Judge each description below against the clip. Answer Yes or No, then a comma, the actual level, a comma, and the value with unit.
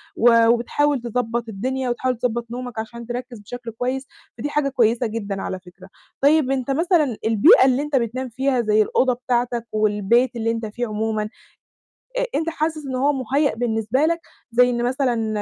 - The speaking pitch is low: No, high, 245 Hz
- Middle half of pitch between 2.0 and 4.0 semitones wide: Yes, average, 2.8 semitones